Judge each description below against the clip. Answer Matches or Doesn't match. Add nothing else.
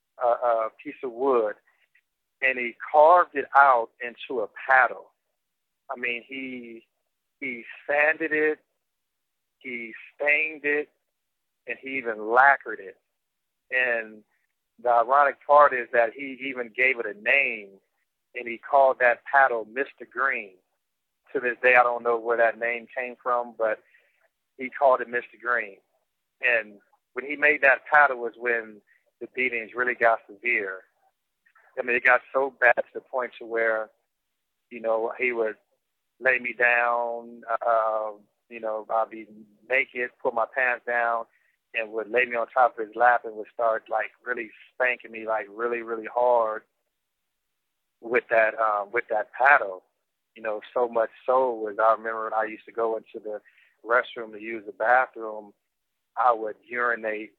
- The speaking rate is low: Doesn't match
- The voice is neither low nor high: Doesn't match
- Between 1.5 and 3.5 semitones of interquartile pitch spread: Matches